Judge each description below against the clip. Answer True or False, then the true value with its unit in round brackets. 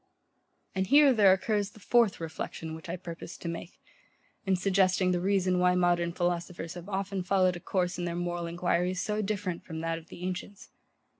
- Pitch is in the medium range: True (180 Hz)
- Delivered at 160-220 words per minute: True (190 wpm)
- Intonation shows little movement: True (1.9 semitones)